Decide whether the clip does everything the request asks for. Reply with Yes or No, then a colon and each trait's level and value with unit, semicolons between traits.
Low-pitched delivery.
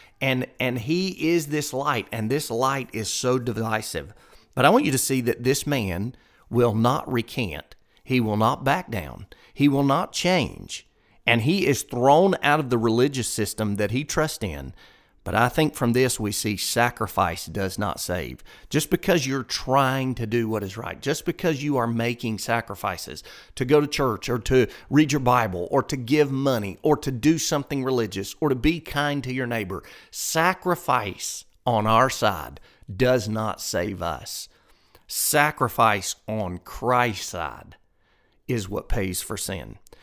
Yes: low, 125 Hz